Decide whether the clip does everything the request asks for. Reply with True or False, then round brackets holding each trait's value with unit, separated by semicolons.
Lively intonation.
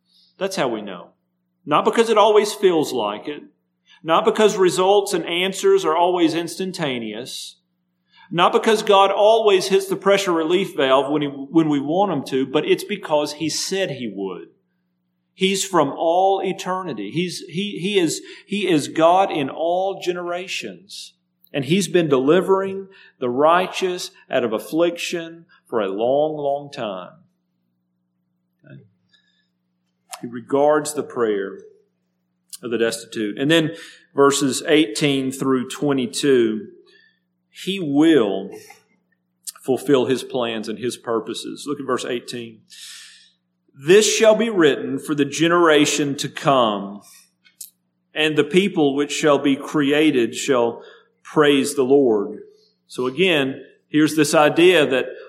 True (7.3 semitones)